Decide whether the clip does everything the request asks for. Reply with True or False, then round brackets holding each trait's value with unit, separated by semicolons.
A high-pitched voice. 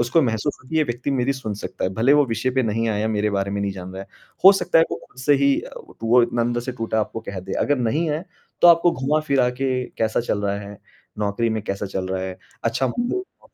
False (120 Hz)